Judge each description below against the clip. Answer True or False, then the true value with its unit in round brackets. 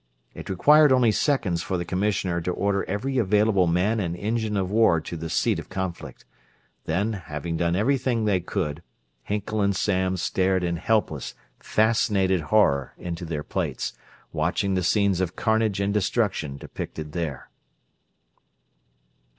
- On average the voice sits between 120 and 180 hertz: False (95 Hz)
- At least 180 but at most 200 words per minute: False (145 wpm)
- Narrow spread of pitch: False (3.8 semitones)